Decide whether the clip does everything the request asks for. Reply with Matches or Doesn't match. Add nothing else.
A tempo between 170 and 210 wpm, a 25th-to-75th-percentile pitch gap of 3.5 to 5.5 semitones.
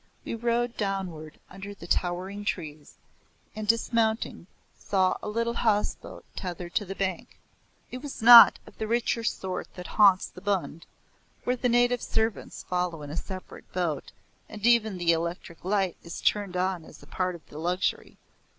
Doesn't match